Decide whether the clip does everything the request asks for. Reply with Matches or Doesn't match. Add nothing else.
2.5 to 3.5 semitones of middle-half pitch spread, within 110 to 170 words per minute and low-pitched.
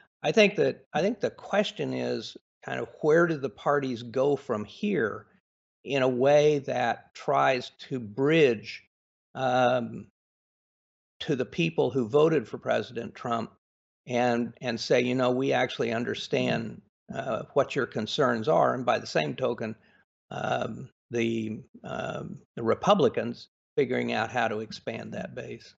Matches